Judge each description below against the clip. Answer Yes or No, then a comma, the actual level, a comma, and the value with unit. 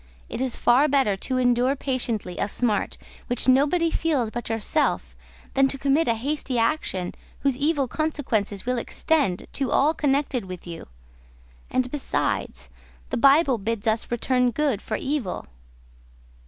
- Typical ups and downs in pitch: Yes, average, 3.9 semitones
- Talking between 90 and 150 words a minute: Yes, average, 145 wpm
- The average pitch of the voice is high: Yes, very high, 255 Hz